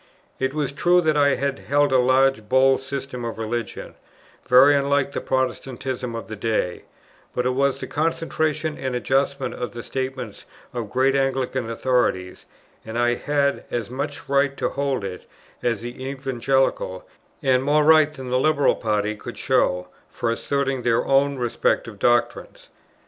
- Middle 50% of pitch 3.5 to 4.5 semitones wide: No, average, 2.7 semitones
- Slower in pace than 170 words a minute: Yes, average, 155 wpm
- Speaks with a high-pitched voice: No, low, 130 Hz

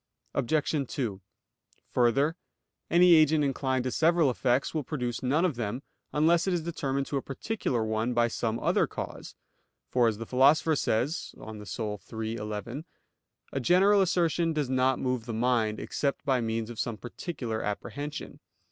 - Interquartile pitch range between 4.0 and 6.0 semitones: Yes, average, 5.0 semitones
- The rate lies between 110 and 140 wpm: No, average, 160 wpm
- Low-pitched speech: Yes, low, 130 Hz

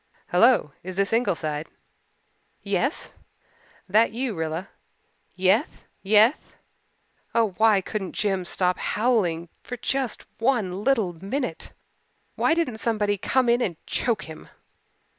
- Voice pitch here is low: No, high, 210 Hz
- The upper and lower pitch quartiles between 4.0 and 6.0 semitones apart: Yes, average, 4.7 semitones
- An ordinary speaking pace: No, slow, 115 wpm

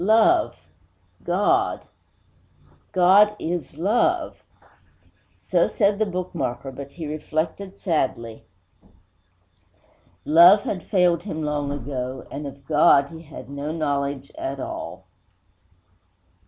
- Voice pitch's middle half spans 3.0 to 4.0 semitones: No, average, 5.1 semitones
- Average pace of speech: No, slow, 105 wpm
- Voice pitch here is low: No, medium, 160 Hz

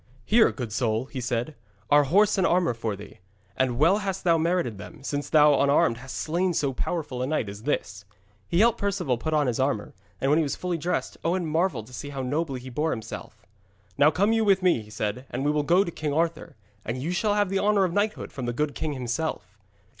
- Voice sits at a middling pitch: Yes, medium, 150 Hz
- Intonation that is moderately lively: No, wide, 5.8 semitones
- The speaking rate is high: Yes, fast, 230 wpm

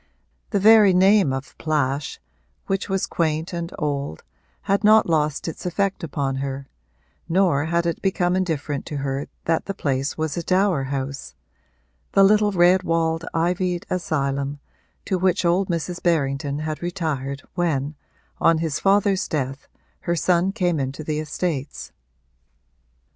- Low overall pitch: No, medium, 165 Hz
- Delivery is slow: No, average, 145 wpm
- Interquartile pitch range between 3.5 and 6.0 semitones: Yes, average, 4.5 semitones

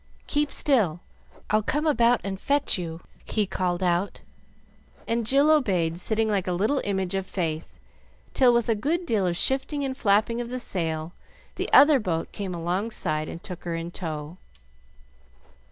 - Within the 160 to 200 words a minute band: Yes, average, 165 wpm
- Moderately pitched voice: No, high, 200 Hz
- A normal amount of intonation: No, wide, 5.9 semitones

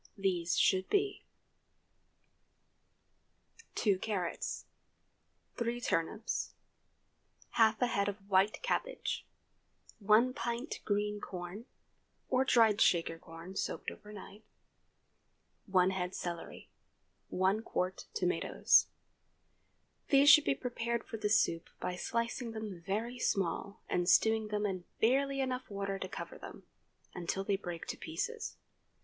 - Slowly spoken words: Yes, slow, 115 wpm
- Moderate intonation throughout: Yes, average, 3.9 semitones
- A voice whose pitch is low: No, high, 210 Hz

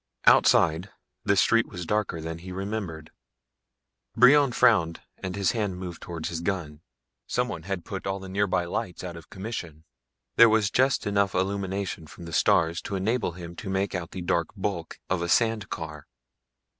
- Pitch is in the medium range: No, very low, 95 Hz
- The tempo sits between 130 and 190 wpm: Yes, average, 170 wpm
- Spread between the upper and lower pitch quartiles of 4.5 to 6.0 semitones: No, average, 3.3 semitones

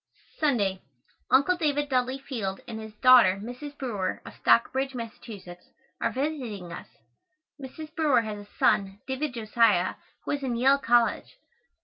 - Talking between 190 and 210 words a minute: No, average, 140 wpm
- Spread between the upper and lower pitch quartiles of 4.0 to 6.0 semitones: Yes, average, 4.5 semitones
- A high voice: Yes, very high, 250 Hz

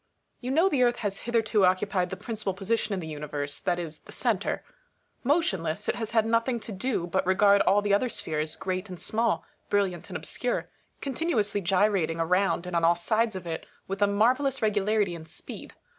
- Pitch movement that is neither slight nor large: Yes, average, 4.0 semitones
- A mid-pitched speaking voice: No, high, 200 Hz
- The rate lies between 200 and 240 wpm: Yes, fast, 205 wpm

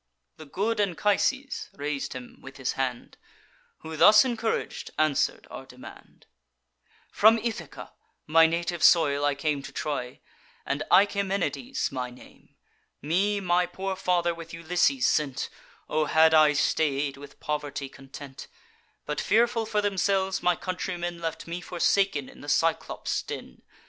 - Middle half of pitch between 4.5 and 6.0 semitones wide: Yes, average, 5.2 semitones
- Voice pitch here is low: No, medium, 165 Hz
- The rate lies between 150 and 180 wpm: No, slow, 135 wpm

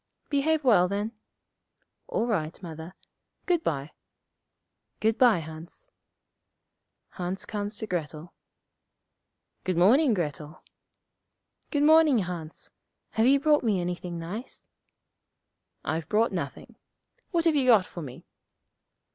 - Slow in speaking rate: Yes, slow, 115 wpm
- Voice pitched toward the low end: No, high, 200 Hz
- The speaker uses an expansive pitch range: Yes, wide, 7.5 semitones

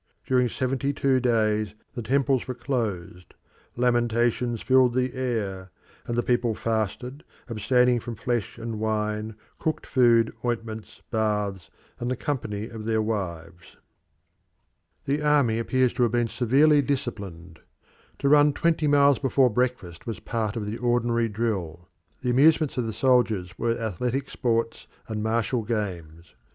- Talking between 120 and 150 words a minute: Yes, average, 140 wpm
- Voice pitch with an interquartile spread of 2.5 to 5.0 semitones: Yes, average, 2.9 semitones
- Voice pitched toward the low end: Yes, low, 115 Hz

